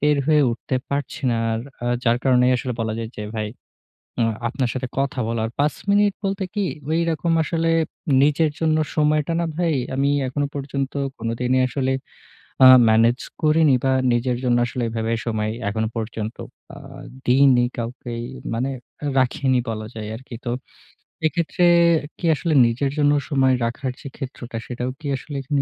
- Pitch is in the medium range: No, low, 130 Hz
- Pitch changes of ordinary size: Yes, average, 4.1 semitones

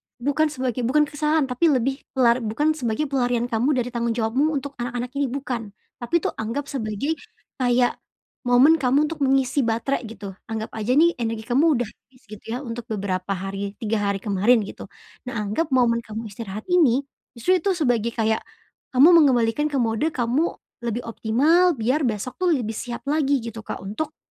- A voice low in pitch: No, high, 245 Hz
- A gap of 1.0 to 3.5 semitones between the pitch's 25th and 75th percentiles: No, average, 4.2 semitones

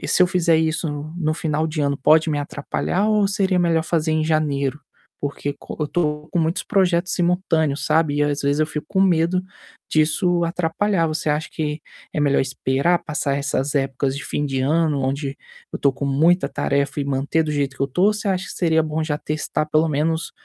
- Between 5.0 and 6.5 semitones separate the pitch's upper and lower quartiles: No, average, 2.9 semitones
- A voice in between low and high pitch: Yes, medium, 155 Hz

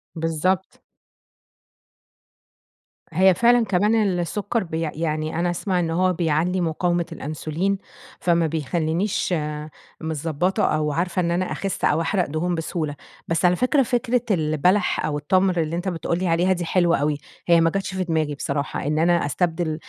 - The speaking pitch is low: No, medium, 170 Hz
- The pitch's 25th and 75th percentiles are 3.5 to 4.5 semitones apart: No, average, 2.8 semitones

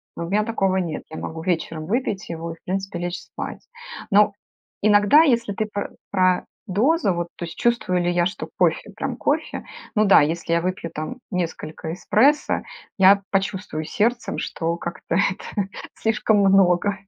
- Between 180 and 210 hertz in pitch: Yes, high, 190 Hz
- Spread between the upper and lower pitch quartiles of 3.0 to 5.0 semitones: Yes, average, 3.3 semitones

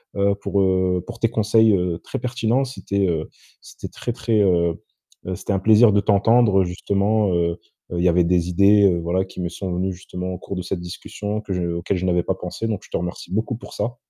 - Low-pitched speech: Yes, very low, 95 Hz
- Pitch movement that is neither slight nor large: Yes, average, 3.2 semitones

